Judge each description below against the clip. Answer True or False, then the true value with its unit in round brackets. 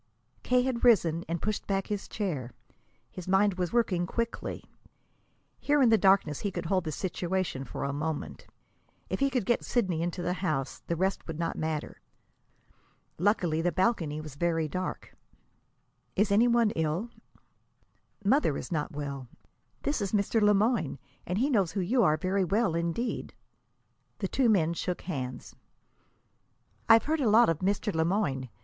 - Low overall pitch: False (185 Hz)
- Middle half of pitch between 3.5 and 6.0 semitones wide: True (4.9 semitones)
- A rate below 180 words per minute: True (165 wpm)